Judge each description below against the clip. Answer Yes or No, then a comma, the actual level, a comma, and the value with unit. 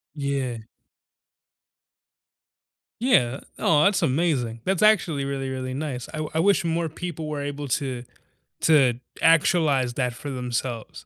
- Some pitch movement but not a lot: Yes, average, 4.1 semitones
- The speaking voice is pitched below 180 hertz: Yes, medium, 140 Hz